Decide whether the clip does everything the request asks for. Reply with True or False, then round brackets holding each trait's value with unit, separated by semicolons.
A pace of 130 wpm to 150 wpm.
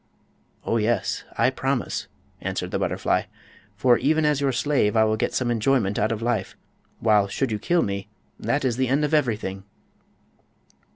False (165 wpm)